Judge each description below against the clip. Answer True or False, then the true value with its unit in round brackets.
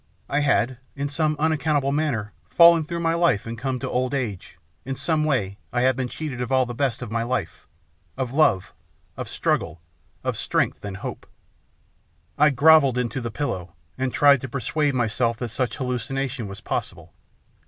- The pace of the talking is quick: False (175 wpm)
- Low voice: True (130 Hz)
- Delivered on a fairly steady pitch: False (3.8 semitones)